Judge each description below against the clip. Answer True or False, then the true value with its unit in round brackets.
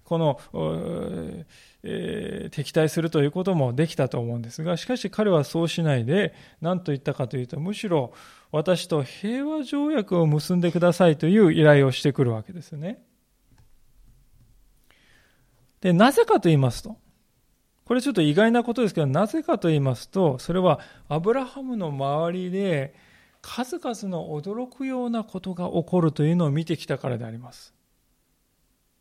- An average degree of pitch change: False (5.9 semitones)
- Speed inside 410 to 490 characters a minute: False (325 characters per minute)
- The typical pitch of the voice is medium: True (170 Hz)